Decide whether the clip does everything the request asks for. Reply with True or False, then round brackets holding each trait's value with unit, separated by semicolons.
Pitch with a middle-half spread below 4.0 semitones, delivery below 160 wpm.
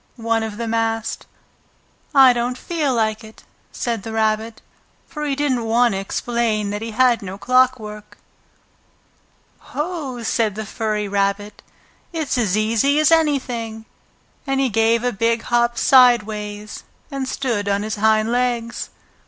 True (2.8 semitones; 145 wpm)